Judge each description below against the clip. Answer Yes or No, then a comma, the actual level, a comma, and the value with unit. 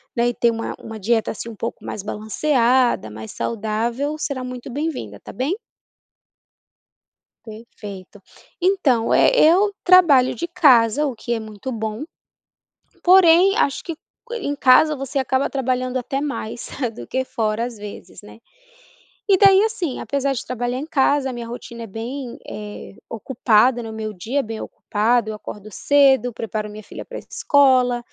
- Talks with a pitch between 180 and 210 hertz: No, high, 245 Hz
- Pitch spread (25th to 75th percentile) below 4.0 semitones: No, average, 4.4 semitones